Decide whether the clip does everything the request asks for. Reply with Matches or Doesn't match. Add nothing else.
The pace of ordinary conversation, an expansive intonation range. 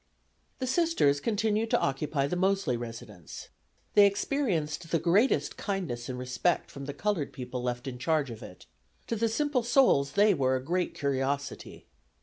Matches